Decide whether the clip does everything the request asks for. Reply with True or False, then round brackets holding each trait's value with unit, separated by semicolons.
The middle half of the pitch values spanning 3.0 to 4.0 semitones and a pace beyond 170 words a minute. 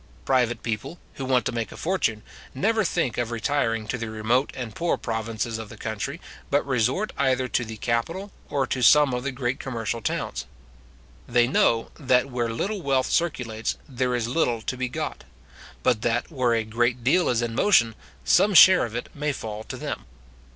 True (3.4 semitones; 190 wpm)